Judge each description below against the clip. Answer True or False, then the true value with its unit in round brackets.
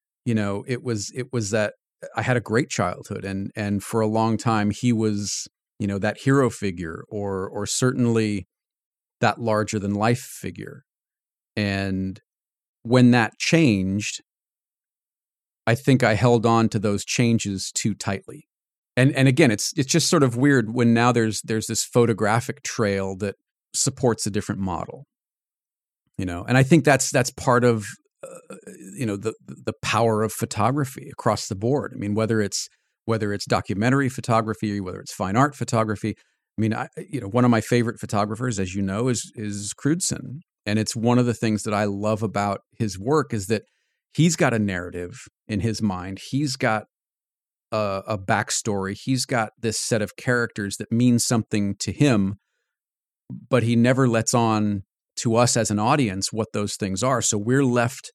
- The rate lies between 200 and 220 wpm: False (175 wpm)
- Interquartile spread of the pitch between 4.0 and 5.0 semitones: False (3.2 semitones)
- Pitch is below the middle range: True (110 Hz)